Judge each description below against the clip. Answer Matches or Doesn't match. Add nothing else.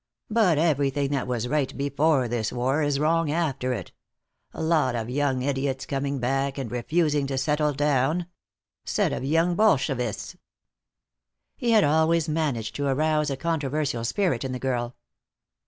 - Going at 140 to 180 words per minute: Matches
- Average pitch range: Matches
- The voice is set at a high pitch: Doesn't match